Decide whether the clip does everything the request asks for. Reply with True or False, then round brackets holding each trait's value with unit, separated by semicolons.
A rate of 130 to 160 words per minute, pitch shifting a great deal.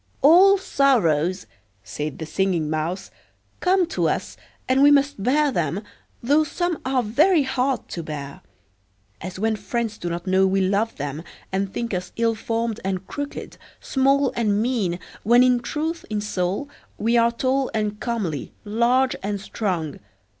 True (155 wpm; 6.1 semitones)